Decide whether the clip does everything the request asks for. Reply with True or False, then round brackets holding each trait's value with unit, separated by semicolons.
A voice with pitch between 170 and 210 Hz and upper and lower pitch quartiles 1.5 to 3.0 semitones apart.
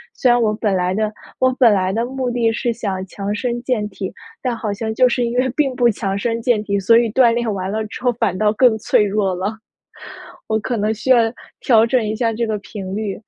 False (220 Hz; 2.7 semitones)